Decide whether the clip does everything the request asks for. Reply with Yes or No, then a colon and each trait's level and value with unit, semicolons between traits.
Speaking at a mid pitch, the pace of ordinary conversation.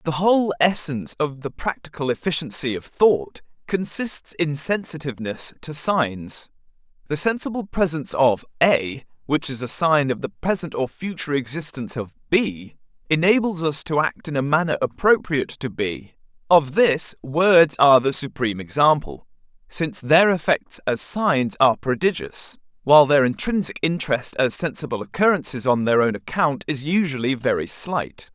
Yes: medium, 150 Hz; average, 150 wpm